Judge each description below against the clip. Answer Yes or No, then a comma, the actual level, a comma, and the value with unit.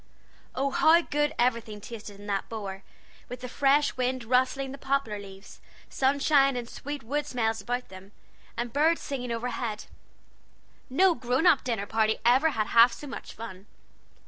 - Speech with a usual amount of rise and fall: Yes, average, 3.8 semitones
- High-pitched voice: Yes, very high, 250 Hz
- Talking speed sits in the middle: Yes, average, 160 wpm